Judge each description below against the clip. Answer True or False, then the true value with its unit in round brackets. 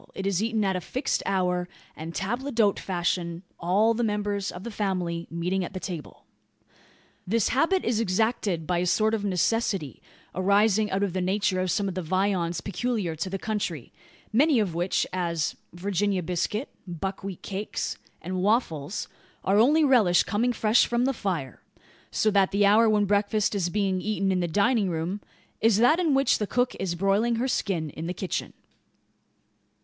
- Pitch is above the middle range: True (195 Hz)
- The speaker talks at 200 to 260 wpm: False (175 wpm)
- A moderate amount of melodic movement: True (3.4 semitones)